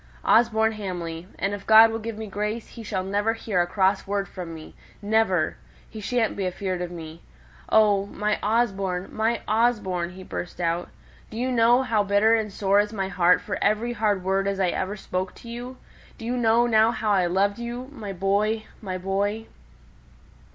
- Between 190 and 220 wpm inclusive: Yes, average, 195 wpm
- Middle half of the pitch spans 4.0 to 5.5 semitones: No, average, 2.9 semitones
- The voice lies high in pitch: Yes, high, 205 Hz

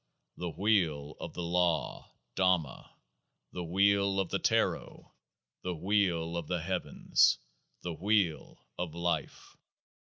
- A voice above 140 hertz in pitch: No, very low, 90 Hz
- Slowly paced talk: Yes, slow, 120 wpm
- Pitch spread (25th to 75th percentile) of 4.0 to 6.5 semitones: No, narrow, 2.6 semitones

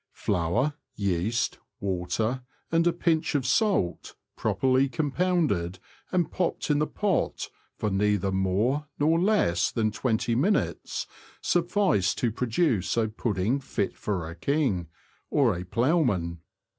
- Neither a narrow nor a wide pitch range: No, wide, 8.5 semitones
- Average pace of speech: No, slow, 130 wpm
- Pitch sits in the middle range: No, low, 120 Hz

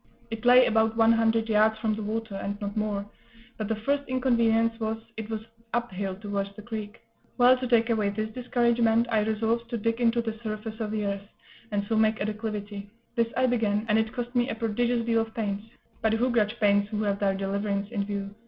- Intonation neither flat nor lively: No, narrow, 1.8 semitones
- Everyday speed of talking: No, fast, 220 wpm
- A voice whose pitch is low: No, high, 220 Hz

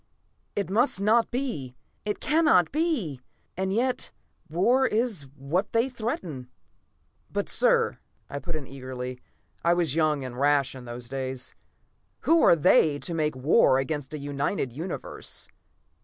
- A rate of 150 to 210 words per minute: No, average, 140 wpm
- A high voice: No, medium, 155 Hz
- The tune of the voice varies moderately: No, wide, 8.0 semitones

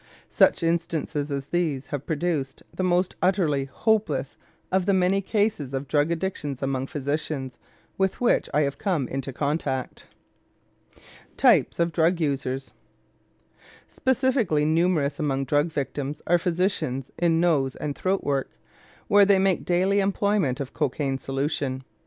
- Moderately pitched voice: Yes, medium, 155 Hz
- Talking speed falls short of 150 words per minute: Yes, slow, 135 wpm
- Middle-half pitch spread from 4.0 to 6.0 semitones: Yes, average, 5.0 semitones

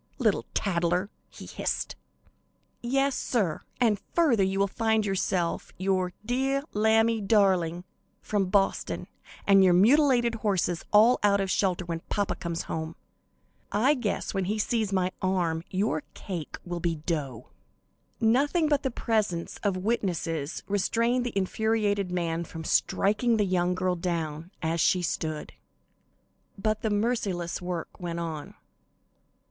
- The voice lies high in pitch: Yes, high, 195 Hz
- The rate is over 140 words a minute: No, slow, 135 wpm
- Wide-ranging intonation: No, average, 4.2 semitones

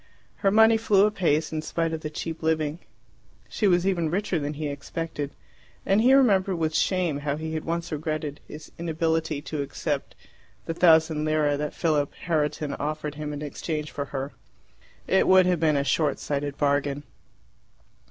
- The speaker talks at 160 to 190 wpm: Yes, average, 165 wpm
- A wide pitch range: No, narrow, 2.5 semitones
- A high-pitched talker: No, medium, 155 Hz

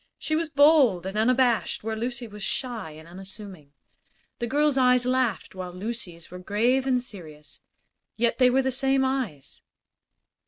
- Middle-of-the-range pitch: No, high, 235 Hz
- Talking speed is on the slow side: No, average, 155 wpm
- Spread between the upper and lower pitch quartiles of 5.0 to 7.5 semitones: Yes, wide, 5.6 semitones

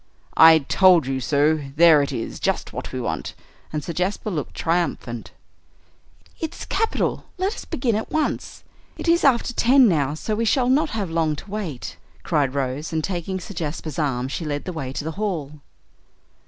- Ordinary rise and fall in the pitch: No, wide, 6.5 semitones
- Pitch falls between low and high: Yes, medium, 165 Hz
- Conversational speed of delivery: Yes, average, 180 wpm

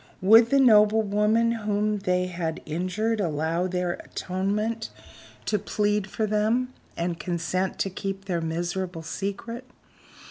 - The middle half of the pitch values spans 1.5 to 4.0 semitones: Yes, average, 3.0 semitones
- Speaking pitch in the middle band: No, high, 195 Hz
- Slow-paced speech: Yes, slow, 130 wpm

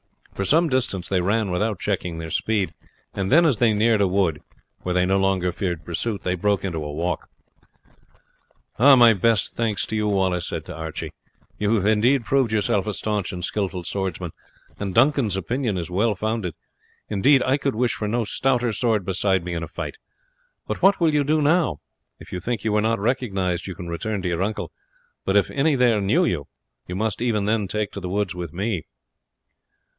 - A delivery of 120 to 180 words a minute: No, average, 200 wpm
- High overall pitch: No, low, 100 Hz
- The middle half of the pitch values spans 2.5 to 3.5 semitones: No, average, 4.2 semitones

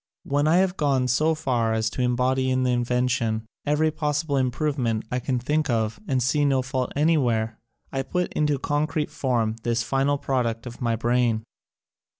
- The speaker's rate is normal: Yes, average, 180 wpm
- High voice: No, low, 130 Hz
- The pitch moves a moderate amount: Yes, average, 3.5 semitones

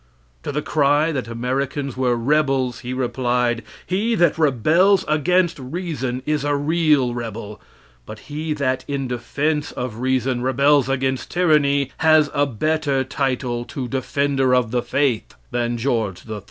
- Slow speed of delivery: No, average, 145 wpm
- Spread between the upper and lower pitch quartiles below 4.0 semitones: Yes, average, 3.4 semitones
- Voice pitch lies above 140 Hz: No, low, 135 Hz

